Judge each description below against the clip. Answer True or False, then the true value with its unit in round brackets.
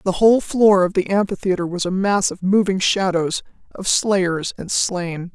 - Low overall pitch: False (190 Hz)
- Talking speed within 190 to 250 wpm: False (180 wpm)